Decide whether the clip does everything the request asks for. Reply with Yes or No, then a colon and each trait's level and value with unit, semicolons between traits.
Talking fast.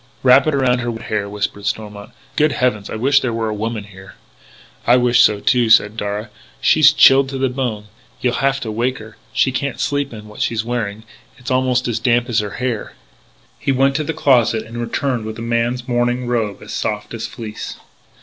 Yes: fast, 210 wpm